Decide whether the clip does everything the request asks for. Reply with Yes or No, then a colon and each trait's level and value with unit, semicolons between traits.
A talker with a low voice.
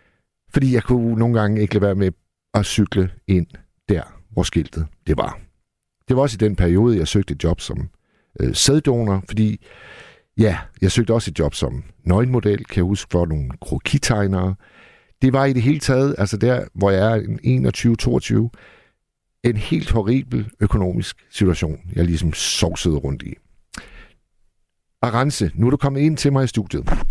Yes: low, 105 Hz